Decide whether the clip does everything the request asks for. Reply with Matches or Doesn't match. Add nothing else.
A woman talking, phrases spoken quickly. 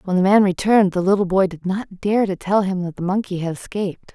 Matches